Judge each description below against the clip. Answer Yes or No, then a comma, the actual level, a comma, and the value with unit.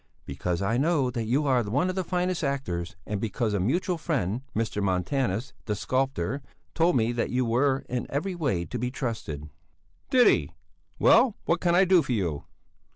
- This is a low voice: Yes, low, 125 Hz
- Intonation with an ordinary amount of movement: No, wide, 6.9 semitones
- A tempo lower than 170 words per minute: No, average, 185 wpm